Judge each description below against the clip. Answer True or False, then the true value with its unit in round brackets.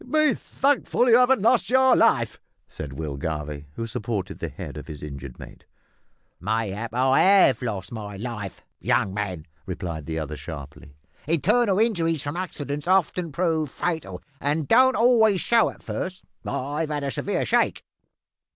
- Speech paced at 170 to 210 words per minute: False (155 wpm)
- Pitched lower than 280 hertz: True (135 Hz)